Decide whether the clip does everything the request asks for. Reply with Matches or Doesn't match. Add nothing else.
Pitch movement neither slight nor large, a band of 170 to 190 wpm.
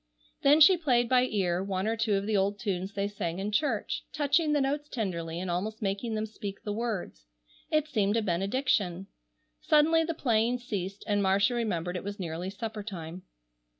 Matches